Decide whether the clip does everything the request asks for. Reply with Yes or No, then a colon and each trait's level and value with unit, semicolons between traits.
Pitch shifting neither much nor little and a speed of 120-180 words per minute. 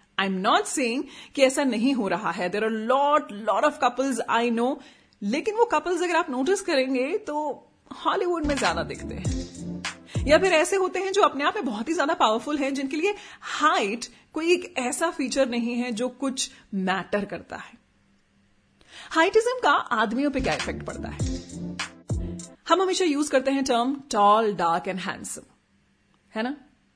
No: wide, 6.1 semitones; average, 175 wpm